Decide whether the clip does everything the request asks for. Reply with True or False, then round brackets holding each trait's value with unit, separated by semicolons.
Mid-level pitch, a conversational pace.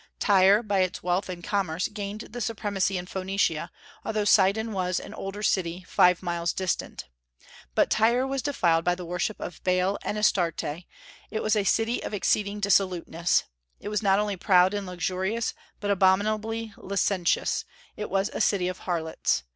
False (195 Hz; 165 wpm)